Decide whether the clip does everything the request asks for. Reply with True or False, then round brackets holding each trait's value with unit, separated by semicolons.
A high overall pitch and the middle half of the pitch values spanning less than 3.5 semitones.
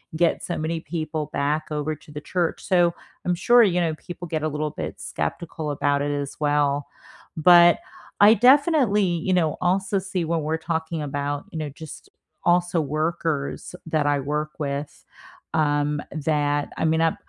False (155 Hz; 2.9 semitones)